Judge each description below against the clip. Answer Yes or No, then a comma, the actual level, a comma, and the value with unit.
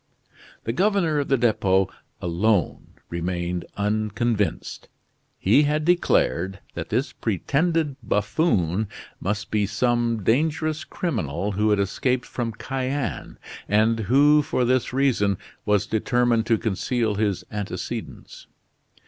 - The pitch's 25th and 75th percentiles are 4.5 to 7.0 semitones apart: Yes, average, 5.1 semitones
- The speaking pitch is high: No, low, 110 Hz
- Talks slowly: Yes, slow, 115 wpm